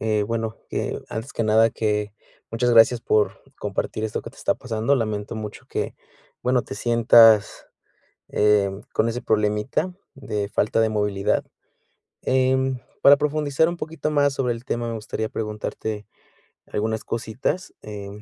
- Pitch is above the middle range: No, low, 115 Hz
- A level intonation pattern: No, average, 3.3 semitones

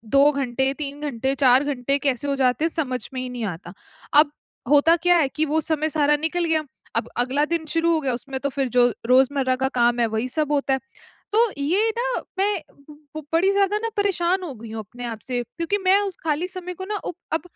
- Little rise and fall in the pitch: No, average, 4.8 semitones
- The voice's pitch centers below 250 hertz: No, very high, 290 Hz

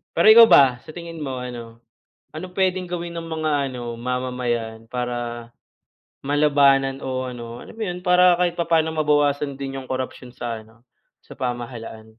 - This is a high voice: No, low, 135 Hz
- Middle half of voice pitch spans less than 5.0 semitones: No, average, 5.3 semitones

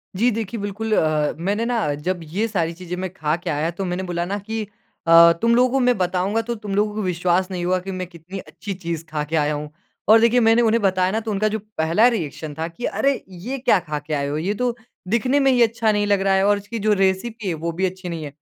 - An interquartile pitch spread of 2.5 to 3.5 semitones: No, average, 4.7 semitones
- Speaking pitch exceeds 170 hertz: Yes, high, 190 Hz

